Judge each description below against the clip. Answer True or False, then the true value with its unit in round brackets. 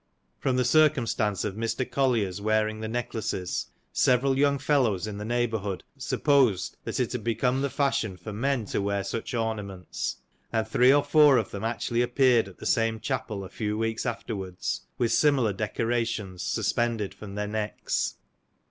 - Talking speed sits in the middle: True (165 wpm)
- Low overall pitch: True (115 Hz)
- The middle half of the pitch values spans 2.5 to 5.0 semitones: True (3.3 semitones)